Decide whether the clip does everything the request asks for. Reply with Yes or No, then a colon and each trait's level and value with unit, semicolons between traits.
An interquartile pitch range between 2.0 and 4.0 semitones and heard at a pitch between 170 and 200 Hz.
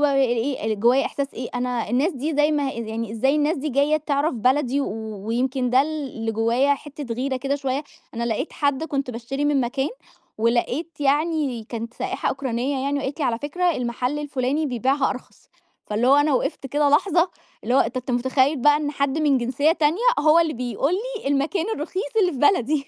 No: average, 3.2 semitones; very high, 275 Hz